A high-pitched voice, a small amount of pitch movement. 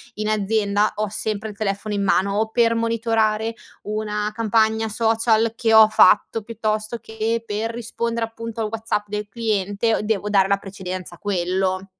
Yes: high, 215 Hz; narrow, 1.7 semitones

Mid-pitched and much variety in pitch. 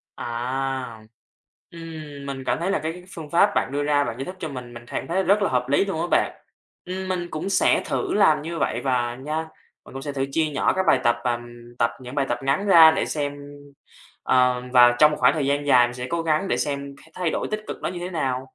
No: medium, 145 Hz; average, 4.7 semitones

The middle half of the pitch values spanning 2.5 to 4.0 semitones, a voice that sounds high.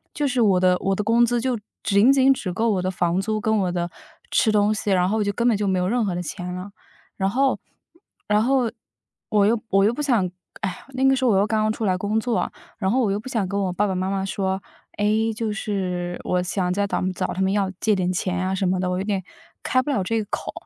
Yes: average, 3.2 semitones; high, 200 Hz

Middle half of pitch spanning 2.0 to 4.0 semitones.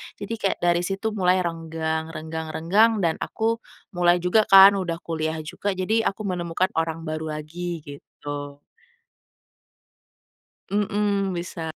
Yes: average, 3.7 semitones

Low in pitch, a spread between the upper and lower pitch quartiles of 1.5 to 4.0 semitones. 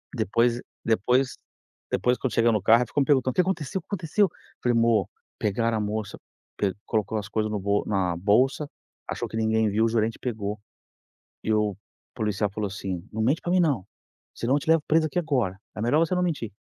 No: low, 115 Hz; average, 4.4 semitones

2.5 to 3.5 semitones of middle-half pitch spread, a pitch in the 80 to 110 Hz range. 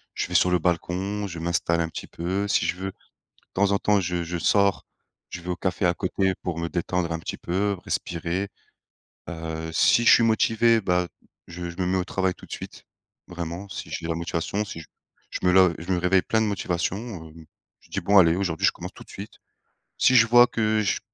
Yes: average, 2.8 semitones; very low, 90 Hz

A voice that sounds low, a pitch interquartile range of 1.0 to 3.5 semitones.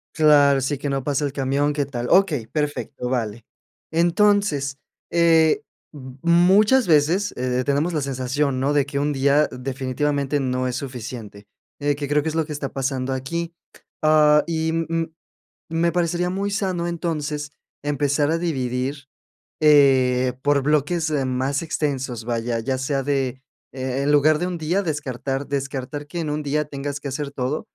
No: medium, 145 Hz; average, 3.1 semitones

